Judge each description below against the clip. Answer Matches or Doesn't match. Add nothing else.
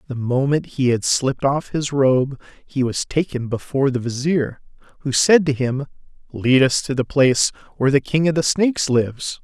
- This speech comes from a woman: Doesn't match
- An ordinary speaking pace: Matches